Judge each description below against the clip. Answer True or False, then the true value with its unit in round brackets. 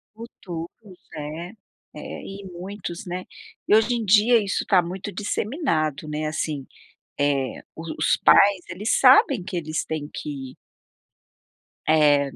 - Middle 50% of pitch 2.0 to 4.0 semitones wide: False (5.0 semitones)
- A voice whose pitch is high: False (175 Hz)